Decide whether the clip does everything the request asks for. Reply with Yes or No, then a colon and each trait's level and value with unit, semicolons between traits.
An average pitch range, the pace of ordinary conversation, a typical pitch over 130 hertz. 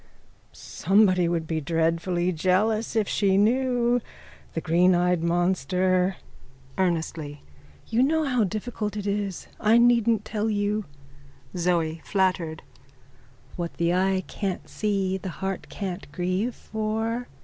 No: average, 3.6 semitones; slow, 120 wpm; high, 190 Hz